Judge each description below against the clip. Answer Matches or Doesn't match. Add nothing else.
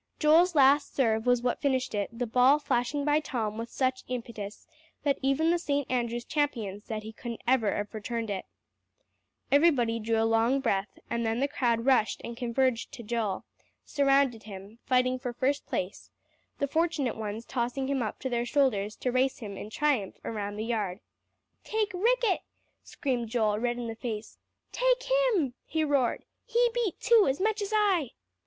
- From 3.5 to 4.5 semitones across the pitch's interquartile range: Matches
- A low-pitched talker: Doesn't match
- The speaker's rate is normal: Matches